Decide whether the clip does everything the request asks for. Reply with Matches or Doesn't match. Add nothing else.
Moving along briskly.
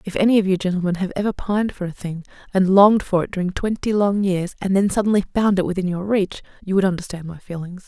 Matches